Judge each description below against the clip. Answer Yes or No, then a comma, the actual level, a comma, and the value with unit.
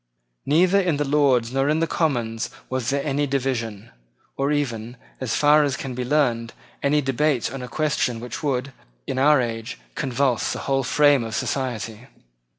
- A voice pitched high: No, low, 135 Hz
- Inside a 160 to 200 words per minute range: Yes, average, 175 wpm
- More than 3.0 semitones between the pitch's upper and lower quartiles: Yes, average, 3.4 semitones